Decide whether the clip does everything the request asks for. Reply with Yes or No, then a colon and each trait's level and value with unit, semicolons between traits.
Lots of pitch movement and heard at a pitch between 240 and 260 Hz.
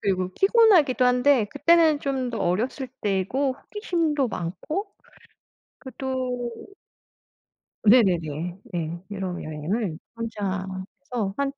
Yes: wide, 6.9 semitones; high, 245 Hz